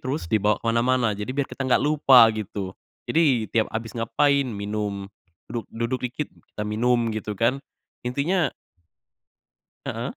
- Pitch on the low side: Yes, low, 115 Hz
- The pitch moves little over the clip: No, average, 3.6 semitones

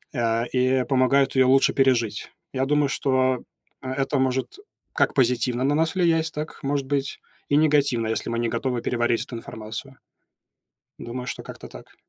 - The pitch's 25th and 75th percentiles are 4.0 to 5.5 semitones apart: No, average, 2.7 semitones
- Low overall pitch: Yes, low, 130 Hz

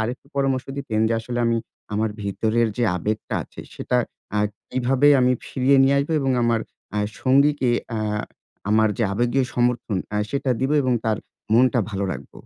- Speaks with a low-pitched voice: Yes, low, 120 Hz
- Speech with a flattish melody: No, average, 3.3 semitones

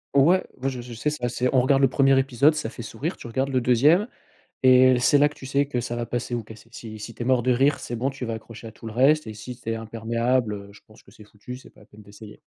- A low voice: Yes, low, 125 Hz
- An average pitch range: Yes, average, 3.0 semitones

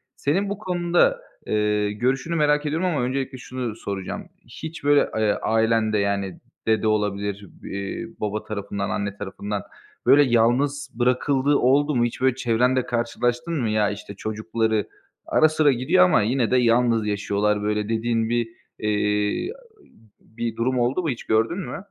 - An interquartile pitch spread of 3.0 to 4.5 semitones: Yes, average, 4.2 semitones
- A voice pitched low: Yes, low, 115 Hz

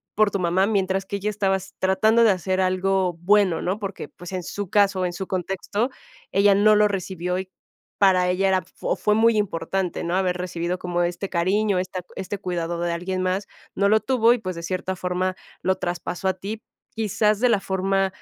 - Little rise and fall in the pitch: Yes, narrow, 2.0 semitones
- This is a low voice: No, high, 190 Hz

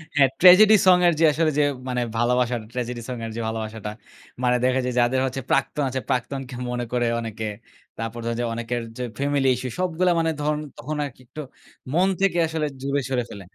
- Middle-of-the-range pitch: No, low, 130 Hz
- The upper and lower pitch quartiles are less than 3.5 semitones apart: No, average, 4.1 semitones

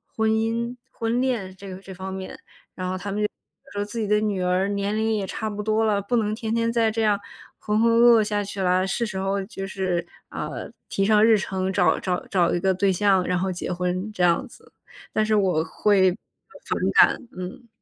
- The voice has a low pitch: No, high, 200 Hz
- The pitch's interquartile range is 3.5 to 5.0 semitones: No, average, 2.7 semitones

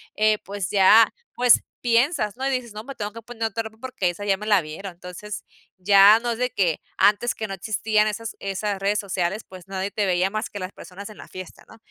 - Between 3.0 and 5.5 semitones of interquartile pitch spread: No, narrow, 2.6 semitones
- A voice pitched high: Yes, high, 210 Hz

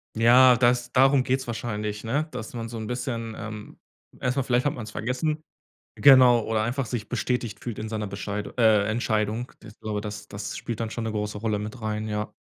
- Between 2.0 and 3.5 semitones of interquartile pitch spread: Yes, narrow, 2.6 semitones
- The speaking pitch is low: Yes, low, 115 Hz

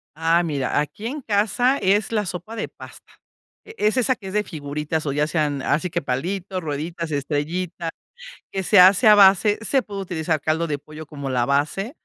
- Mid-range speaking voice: Yes, medium, 170 Hz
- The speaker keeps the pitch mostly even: No, average, 5.2 semitones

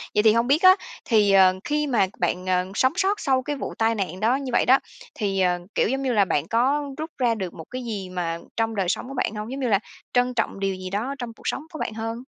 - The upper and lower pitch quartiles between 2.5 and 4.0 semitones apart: No, average, 5.2 semitones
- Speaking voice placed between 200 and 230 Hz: Yes, high, 225 Hz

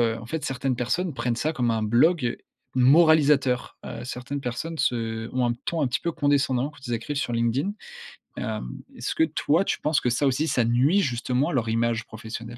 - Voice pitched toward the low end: Yes, low, 130 Hz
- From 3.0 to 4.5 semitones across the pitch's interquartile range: Yes, average, 4.1 semitones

